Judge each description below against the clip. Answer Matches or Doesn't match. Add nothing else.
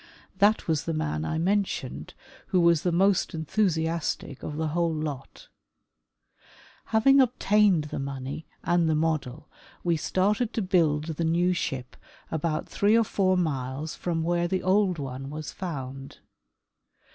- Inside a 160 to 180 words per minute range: Doesn't match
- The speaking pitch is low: Doesn't match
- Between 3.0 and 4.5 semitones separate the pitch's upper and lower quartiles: Matches